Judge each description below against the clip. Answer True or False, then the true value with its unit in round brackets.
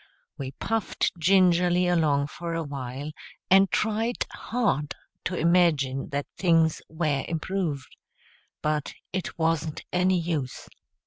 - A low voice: False (165 Hz)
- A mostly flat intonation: False (3.8 semitones)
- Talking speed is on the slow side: True (115 wpm)